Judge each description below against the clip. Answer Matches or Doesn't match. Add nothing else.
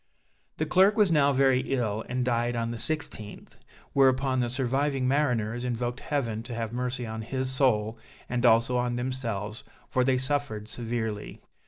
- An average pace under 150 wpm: Doesn't match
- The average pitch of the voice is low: Matches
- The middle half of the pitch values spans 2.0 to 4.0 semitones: Matches